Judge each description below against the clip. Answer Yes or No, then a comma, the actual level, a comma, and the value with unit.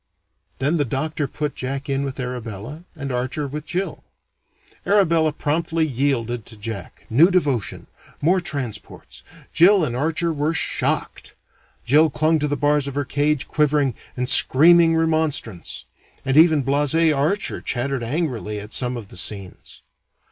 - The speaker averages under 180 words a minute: Yes, average, 145 wpm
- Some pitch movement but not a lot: Yes, average, 3.9 semitones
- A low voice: No, medium, 145 Hz